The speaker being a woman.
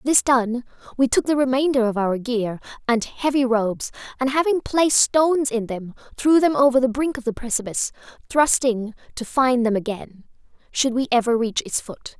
Yes: female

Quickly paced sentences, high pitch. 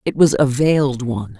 No: fast, 215 wpm; low, 135 Hz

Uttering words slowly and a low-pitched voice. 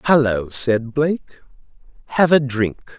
Yes: slow, 120 wpm; low, 130 Hz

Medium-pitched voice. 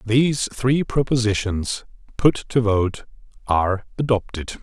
No: low, 115 Hz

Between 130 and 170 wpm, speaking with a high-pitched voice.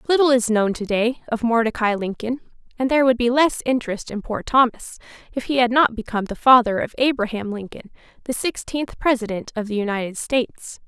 No: average, 180 wpm; high, 235 Hz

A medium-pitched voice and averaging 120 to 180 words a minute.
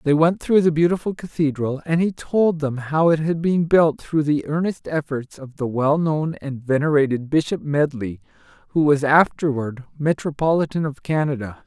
Yes: medium, 150 Hz; average, 165 wpm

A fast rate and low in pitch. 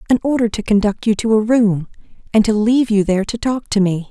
No: fast, 250 wpm; high, 215 Hz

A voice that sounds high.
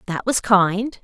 Yes: high, 205 Hz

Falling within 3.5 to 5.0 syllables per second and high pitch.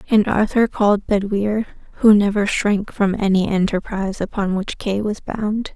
Yes: 4.7 syllables/s; high, 205 Hz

